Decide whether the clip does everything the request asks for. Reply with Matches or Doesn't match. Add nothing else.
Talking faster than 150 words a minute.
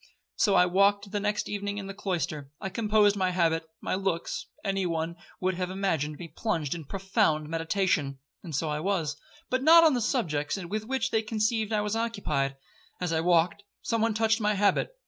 Matches